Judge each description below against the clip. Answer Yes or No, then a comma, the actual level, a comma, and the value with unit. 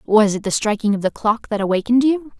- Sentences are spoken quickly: Yes, fast, 250 wpm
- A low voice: No, high, 220 Hz